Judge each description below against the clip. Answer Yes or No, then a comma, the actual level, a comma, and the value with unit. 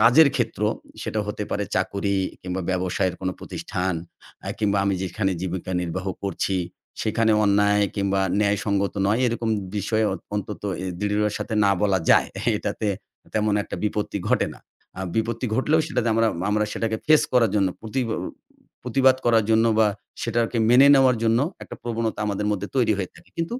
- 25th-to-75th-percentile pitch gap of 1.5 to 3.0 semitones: Yes, average, 2.7 semitones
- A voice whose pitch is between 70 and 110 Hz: Yes, low, 105 Hz